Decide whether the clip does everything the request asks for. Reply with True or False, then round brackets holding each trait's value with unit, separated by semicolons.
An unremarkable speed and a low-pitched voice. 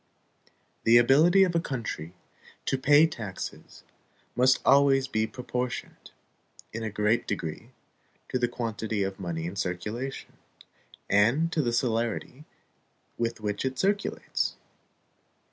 False (120 wpm; 120 Hz)